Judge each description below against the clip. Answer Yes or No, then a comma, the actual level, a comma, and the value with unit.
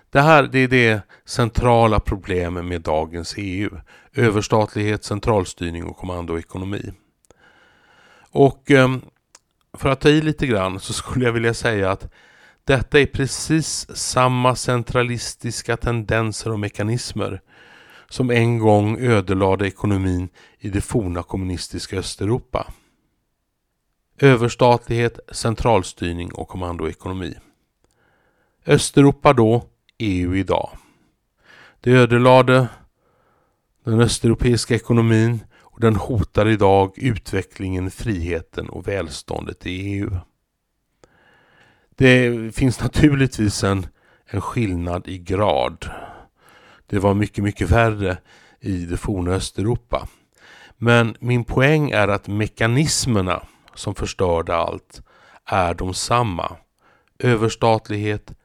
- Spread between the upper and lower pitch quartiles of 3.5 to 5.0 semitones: Yes, average, 4.2 semitones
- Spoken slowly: Yes, slow, 100 wpm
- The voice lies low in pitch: Yes, low, 110 Hz